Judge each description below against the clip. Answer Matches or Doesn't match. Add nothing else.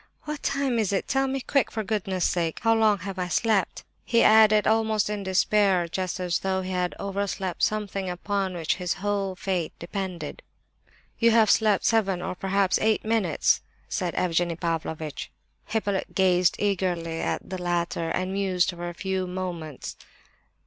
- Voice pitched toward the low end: Doesn't match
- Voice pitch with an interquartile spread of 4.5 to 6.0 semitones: Doesn't match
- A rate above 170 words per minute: Doesn't match